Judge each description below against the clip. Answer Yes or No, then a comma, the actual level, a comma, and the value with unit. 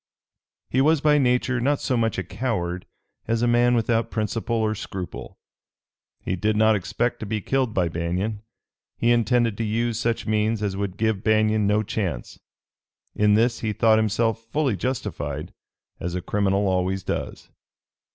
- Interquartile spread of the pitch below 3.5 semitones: Yes, average, 2.8 semitones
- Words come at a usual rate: Yes, average, 160 wpm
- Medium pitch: No, low, 110 Hz